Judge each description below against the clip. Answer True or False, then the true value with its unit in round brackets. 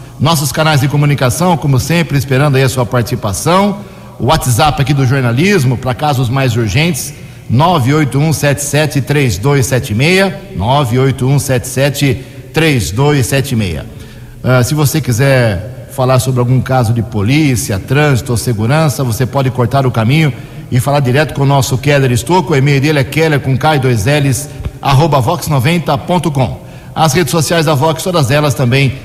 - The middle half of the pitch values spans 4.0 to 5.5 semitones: False (2.9 semitones)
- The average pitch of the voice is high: False (135 Hz)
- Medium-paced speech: True (130 wpm)